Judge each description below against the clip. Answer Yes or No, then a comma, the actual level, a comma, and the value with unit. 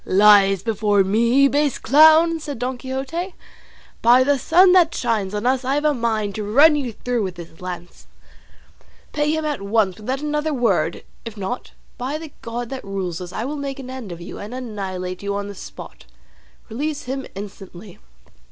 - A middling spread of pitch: No, wide, 5.9 semitones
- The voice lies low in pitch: No, high, 240 Hz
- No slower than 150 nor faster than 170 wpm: No, average, 185 wpm